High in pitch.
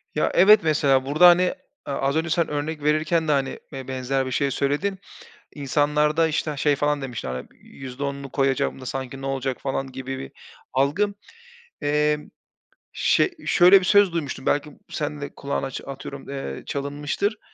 No: medium, 145 Hz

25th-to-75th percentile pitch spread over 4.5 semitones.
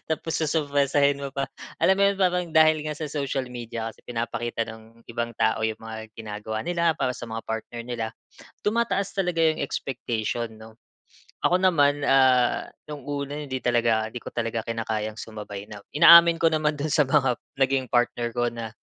Yes: average, 4.9 semitones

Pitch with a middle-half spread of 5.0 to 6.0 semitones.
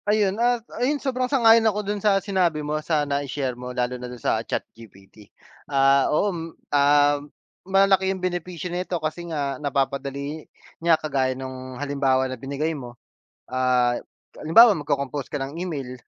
Yes: wide, 5.6 semitones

